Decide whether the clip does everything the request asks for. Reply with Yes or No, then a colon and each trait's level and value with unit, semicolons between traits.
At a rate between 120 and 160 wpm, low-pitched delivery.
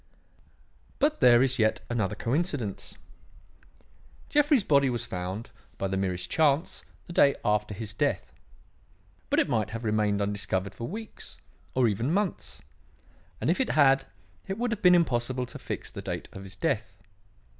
Yes: average, 155 wpm; low, 120 Hz